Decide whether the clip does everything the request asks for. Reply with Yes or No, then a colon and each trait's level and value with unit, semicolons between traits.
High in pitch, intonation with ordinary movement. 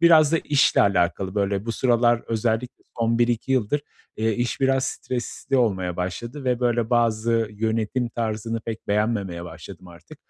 No: low, 115 Hz; average, 3.0 semitones